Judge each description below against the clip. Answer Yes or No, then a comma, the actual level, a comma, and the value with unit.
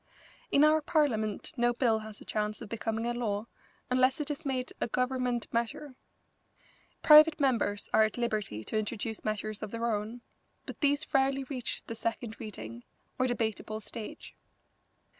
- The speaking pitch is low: No, high, 235 Hz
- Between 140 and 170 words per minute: Yes, average, 160 wpm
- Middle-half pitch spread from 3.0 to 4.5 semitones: Yes, average, 3.4 semitones